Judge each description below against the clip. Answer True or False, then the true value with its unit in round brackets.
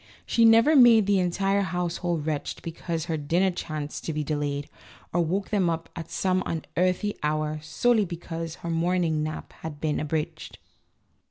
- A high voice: False (170 Hz)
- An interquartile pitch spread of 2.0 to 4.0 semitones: True (3.3 semitones)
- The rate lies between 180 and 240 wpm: False (165 wpm)